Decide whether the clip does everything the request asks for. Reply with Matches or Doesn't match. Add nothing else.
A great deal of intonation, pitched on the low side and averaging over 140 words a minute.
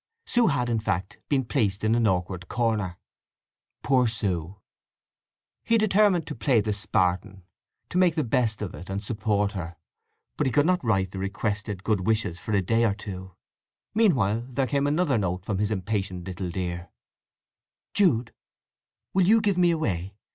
Matches